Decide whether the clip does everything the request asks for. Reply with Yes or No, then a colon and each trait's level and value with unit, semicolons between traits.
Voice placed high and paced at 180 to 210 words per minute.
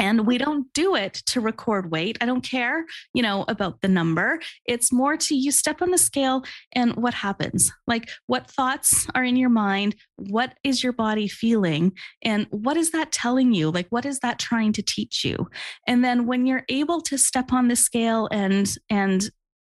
Yes: high, 240 Hz; average, 200 wpm